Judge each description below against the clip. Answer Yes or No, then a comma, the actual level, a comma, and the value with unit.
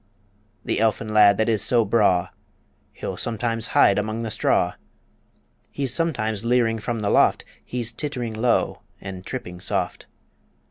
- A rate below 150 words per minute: Yes, average, 140 wpm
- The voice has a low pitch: Yes, low, 110 Hz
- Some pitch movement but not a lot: No, narrow, 2.1 semitones